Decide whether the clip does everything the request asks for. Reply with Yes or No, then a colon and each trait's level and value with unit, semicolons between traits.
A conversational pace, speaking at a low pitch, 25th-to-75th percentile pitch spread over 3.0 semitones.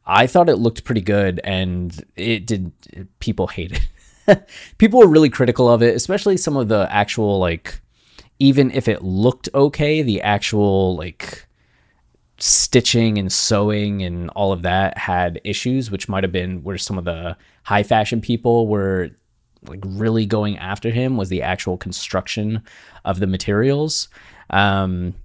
Yes: average, 155 wpm; low, 100 Hz; average, 4.1 semitones